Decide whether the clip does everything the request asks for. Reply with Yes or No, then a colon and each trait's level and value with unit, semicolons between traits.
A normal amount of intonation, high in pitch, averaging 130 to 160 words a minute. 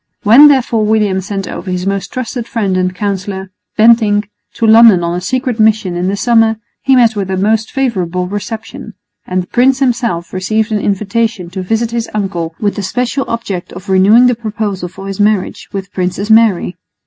No: average, 3.4 semitones; high, 205 Hz; average, 190 wpm